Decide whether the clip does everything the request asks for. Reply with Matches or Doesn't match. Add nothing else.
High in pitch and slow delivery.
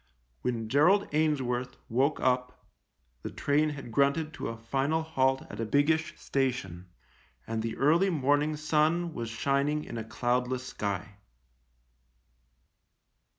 Doesn't match